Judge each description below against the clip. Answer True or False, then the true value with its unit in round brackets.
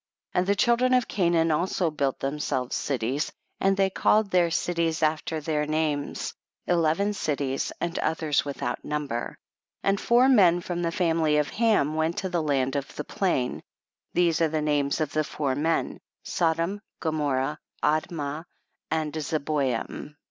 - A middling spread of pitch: True (3.1 semitones)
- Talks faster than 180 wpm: False (155 wpm)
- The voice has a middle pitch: True (160 Hz)